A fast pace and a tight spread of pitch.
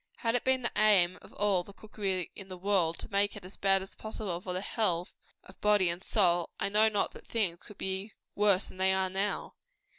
Yes: fast, 235 wpm; narrow, 2.3 semitones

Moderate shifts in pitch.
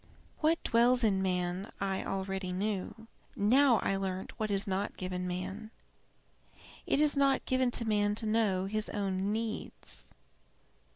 Yes: average, 3.1 semitones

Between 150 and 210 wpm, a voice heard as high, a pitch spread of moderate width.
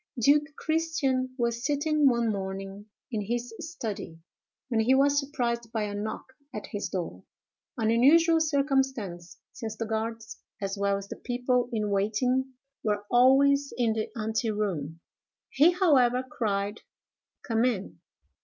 No: slow, 135 wpm; high, 235 Hz; average, 4.4 semitones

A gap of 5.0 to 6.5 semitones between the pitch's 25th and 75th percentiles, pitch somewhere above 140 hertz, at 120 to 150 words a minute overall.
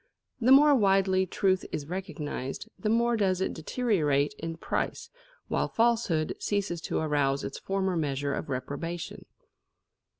Yes: wide, 5.5 semitones; medium, 185 Hz; slow, 135 wpm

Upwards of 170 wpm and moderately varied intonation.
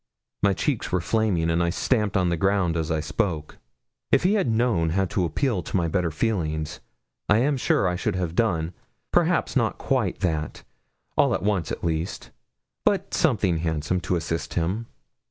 Yes: average, 180 wpm; average, 3.9 semitones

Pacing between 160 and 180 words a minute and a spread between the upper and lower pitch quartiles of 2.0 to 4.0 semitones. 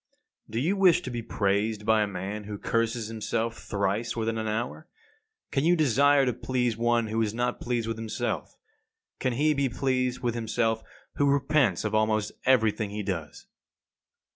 Yes: average, 175 wpm; average, 2.9 semitones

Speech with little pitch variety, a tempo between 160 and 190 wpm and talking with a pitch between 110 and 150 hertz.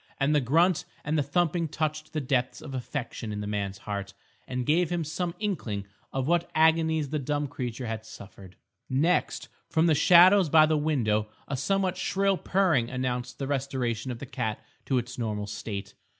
No: average, 5.3 semitones; average, 180 wpm; medium, 140 Hz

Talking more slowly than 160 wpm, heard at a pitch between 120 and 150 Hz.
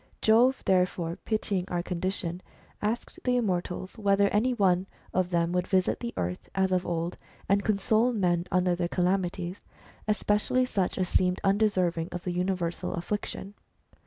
No: average, 150 wpm; medium, 185 Hz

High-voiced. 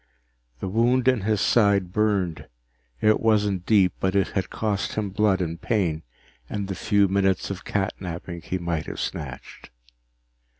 No: low, 100 Hz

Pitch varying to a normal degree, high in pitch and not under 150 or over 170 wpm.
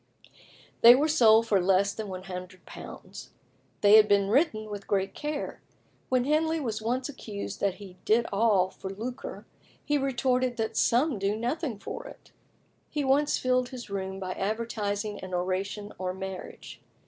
Yes: average, 4.6 semitones; high, 215 Hz; average, 155 wpm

